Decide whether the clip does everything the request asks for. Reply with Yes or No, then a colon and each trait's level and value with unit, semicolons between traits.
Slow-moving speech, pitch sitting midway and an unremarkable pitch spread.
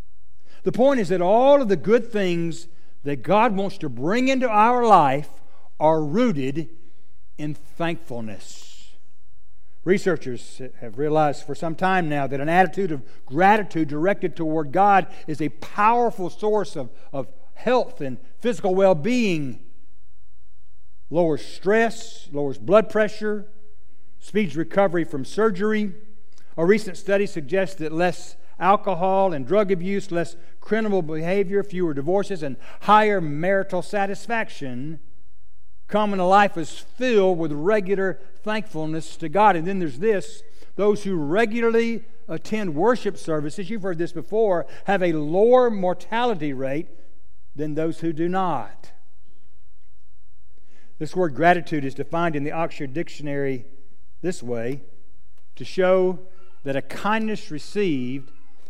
No: slow, 130 wpm; medium, 170 Hz; wide, 6.3 semitones